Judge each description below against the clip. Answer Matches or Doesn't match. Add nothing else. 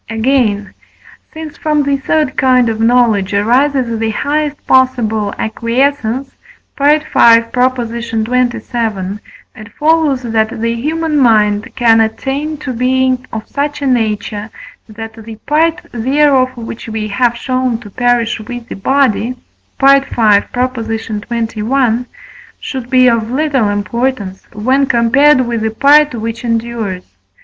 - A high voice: Matches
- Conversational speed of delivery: Doesn't match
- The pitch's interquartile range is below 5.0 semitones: Matches